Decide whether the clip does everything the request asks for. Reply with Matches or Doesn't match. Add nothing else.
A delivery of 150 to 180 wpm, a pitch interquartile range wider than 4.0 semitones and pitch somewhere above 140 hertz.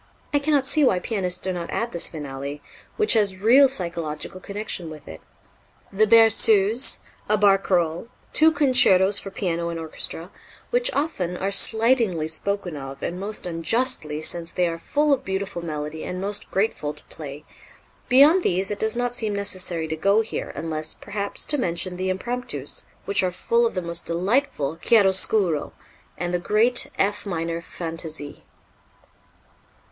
Matches